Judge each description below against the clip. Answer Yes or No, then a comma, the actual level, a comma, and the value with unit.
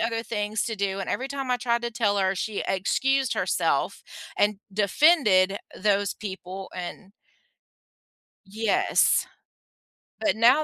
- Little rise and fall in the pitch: No, average, 3.5 semitones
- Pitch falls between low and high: No, high, 210 Hz